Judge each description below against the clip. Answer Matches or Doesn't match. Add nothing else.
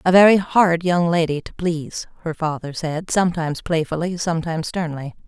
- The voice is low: Doesn't match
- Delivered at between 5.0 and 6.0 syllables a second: Matches